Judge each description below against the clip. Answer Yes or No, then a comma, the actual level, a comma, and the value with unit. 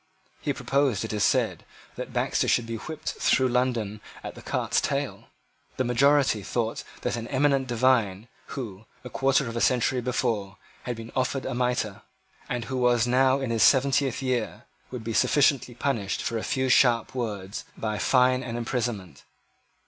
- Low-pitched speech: Yes, low, 125 Hz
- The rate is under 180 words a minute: Yes, average, 170 wpm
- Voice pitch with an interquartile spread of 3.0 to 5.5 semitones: No, narrow, 2.6 semitones